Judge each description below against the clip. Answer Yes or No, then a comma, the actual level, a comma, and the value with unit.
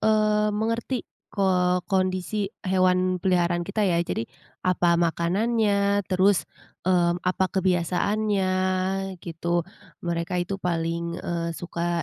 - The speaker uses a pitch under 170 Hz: No, medium, 185 Hz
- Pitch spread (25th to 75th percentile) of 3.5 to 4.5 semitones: No, average, 2.7 semitones